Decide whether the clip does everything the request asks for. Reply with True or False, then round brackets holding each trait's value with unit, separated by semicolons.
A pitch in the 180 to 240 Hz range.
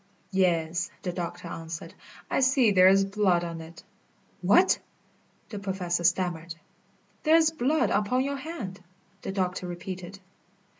True (185 Hz)